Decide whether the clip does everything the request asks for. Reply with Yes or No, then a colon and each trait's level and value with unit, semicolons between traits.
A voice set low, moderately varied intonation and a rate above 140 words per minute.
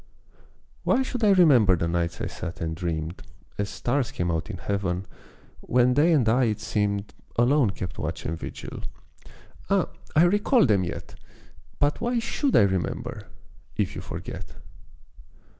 No: low, 105 Hz; wide, 8.6 semitones; average, 155 wpm